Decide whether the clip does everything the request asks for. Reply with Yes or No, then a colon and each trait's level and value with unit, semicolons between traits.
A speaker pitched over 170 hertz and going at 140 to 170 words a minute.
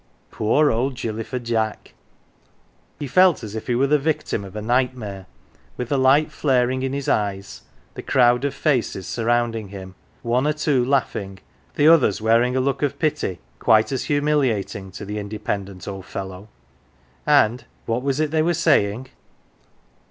No: low, 120 Hz; average, 165 wpm